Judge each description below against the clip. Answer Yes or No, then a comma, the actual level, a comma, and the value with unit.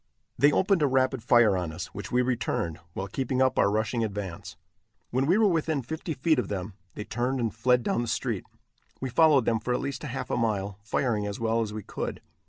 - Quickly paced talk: Yes, fast, 220 wpm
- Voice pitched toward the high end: No, low, 120 Hz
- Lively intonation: No, average, 4.1 semitones